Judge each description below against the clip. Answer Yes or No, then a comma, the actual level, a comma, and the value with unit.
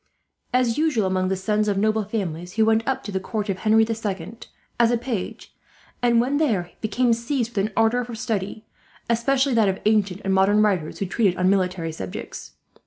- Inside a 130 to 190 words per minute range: No, average, 200 wpm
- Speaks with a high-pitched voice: Yes, high, 215 Hz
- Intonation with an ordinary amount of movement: Yes, average, 3.4 semitones